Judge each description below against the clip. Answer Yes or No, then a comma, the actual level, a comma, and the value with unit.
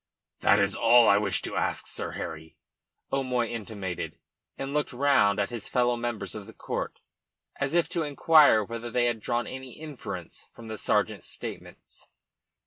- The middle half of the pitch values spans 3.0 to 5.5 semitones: Yes, average, 4.3 semitones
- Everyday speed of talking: Yes, average, 165 wpm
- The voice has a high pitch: No, low, 120 Hz